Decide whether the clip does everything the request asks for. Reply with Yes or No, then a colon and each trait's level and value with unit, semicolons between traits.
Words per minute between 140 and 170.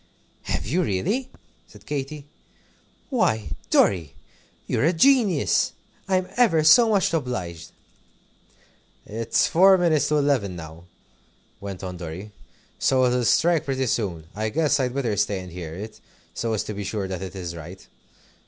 Yes: average, 150 wpm